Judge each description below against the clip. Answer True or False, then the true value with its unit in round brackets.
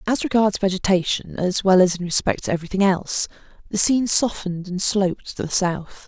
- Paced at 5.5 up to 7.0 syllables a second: True (5.8 syllables/s)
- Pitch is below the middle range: False (190 Hz)